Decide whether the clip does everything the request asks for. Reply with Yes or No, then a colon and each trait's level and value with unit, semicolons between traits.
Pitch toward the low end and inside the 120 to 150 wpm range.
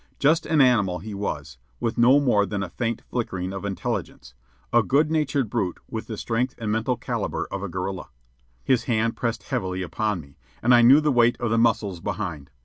No: low, 110 Hz; average, 200 wpm